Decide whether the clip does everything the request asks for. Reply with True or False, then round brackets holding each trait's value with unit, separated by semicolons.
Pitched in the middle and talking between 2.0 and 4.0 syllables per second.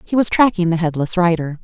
False (180 Hz; 5.9 syllables/s)